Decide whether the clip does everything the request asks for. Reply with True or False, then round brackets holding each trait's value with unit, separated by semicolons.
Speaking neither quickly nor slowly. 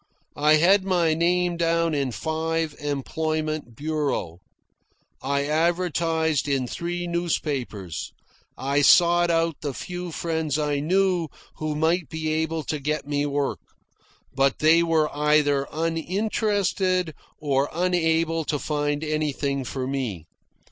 False (120 wpm)